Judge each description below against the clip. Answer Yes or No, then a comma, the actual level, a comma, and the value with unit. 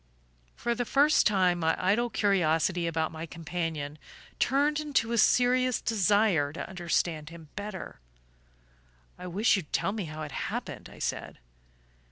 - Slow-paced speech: No, average, 145 wpm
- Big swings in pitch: Yes, wide, 5.8 semitones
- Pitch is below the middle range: No, medium, 185 Hz